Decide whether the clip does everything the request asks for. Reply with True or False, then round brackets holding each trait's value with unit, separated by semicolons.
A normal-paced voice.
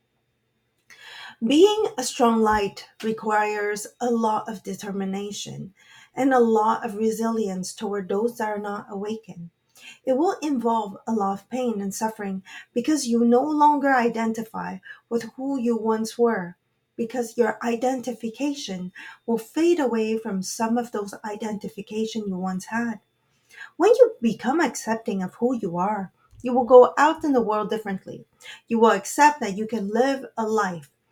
True (150 wpm)